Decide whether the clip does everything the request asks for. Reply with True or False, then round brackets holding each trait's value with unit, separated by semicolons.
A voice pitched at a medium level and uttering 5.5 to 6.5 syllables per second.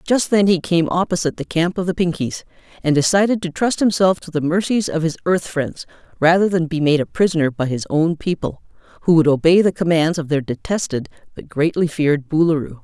True (165 Hz; 5.8 syllables/s)